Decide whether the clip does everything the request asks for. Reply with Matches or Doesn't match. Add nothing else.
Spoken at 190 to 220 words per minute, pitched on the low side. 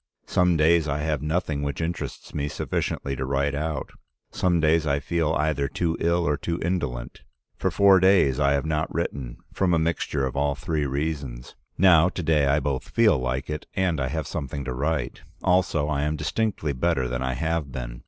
Matches